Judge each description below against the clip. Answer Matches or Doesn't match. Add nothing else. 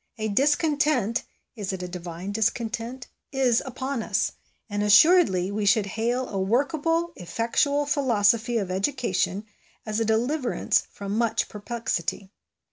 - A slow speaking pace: Matches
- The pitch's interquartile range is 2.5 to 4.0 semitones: Doesn't match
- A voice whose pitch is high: Matches